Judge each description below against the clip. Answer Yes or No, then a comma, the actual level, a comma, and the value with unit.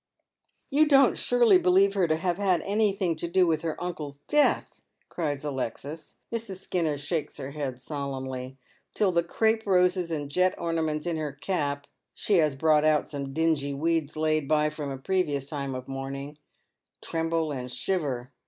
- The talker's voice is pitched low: No, medium, 155 Hz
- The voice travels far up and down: No, average, 4.2 semitones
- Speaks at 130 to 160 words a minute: No, average, 180 wpm